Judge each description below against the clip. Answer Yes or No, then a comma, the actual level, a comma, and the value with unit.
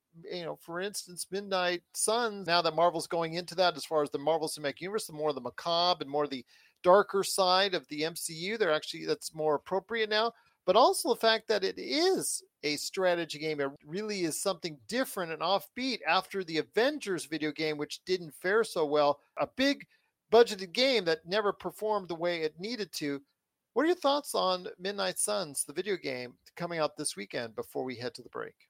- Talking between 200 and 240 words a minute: Yes, fast, 205 wpm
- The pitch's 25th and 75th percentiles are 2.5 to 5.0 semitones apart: No, wide, 5.6 semitones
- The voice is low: No, medium, 175 Hz